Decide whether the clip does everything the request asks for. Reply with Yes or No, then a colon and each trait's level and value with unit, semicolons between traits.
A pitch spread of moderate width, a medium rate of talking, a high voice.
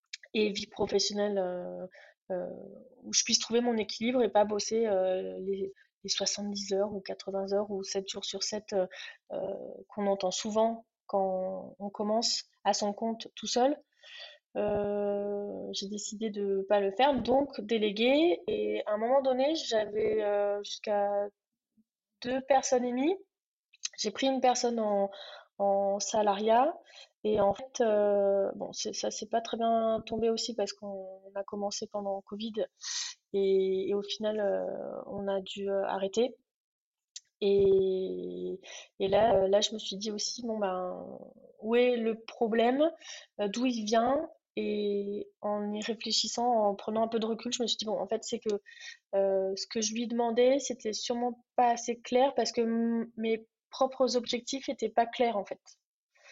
Yes: average, 3.2 semitones; average, 165 wpm; high, 215 Hz